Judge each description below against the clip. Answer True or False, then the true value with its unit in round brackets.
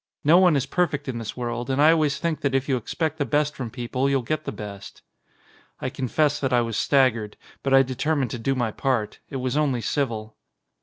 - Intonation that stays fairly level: False (3.5 semitones)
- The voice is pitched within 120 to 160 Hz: True (135 Hz)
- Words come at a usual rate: False (220 wpm)